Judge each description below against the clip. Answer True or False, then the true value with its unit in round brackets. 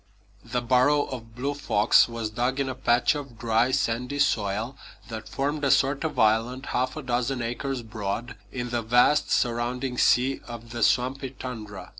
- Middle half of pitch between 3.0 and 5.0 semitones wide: False (2.5 semitones)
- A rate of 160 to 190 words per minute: True (170 wpm)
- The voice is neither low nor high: False (125 Hz)